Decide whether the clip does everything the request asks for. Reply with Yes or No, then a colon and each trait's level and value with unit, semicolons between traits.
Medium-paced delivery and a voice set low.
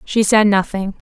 No: average, 170 wpm; high, 205 Hz